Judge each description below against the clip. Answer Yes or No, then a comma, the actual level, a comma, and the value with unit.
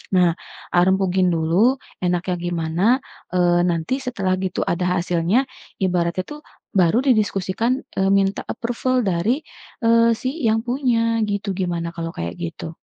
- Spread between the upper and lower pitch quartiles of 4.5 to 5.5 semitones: Yes, average, 4.9 semitones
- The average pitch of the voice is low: No, medium, 185 Hz